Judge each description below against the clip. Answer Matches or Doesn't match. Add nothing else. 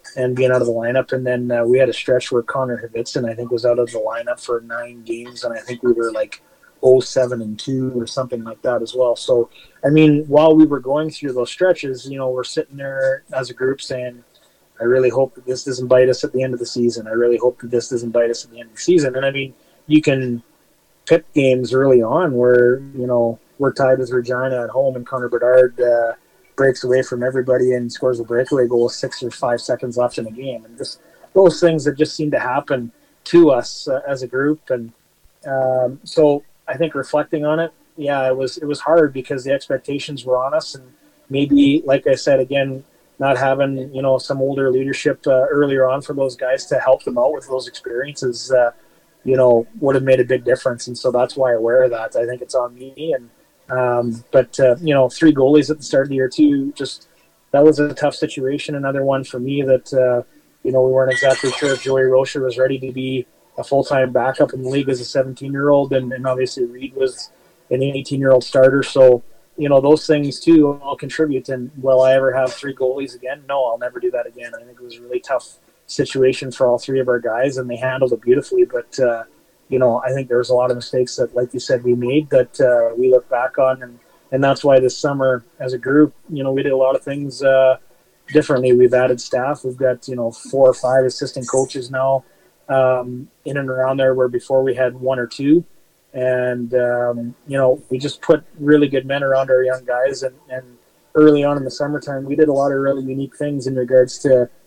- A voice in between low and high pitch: Doesn't match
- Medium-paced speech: Doesn't match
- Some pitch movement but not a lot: Doesn't match